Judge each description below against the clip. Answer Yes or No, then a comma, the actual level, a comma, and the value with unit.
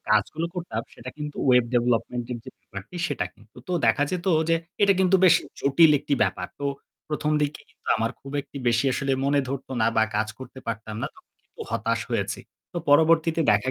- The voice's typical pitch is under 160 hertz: Yes, low, 135 Hz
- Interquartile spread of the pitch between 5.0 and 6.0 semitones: Yes, wide, 5.4 semitones